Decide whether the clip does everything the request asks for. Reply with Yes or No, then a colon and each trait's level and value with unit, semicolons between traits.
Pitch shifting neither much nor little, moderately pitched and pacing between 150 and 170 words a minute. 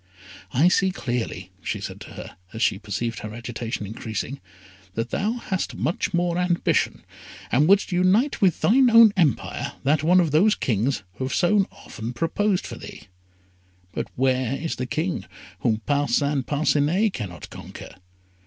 No: wide, 7.4 semitones; medium, 150 Hz; average, 160 wpm